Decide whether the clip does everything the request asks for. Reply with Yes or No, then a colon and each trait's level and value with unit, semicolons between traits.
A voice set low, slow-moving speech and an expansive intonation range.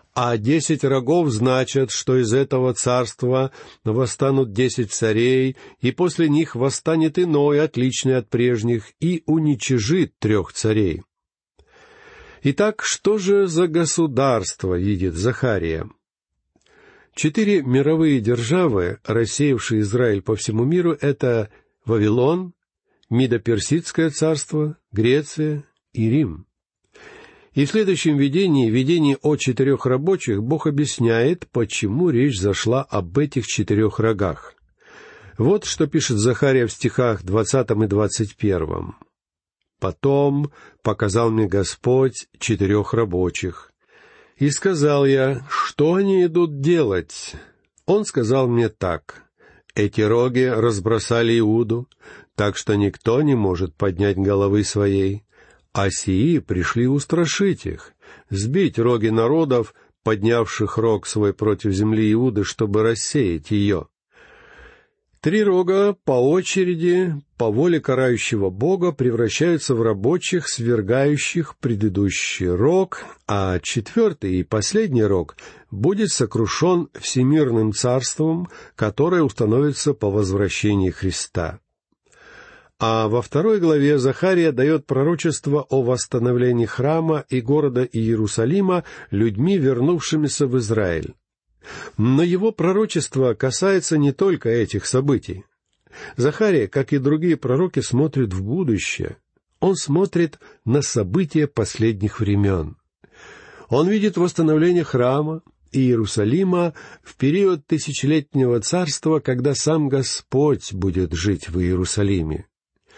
Yes: low, 130 Hz; slow, 105 wpm; wide, 6.0 semitones